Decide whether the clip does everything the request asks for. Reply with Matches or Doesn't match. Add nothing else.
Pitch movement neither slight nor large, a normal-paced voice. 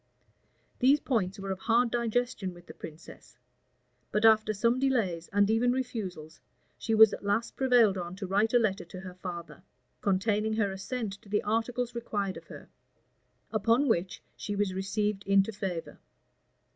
Matches